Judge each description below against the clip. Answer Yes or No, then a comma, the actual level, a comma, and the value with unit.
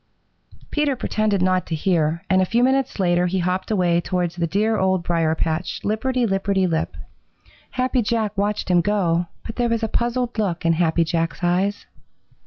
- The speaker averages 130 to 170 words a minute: No, average, 180 wpm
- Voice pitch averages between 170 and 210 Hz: Yes, high, 190 Hz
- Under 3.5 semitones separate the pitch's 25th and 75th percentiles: No, average, 4.1 semitones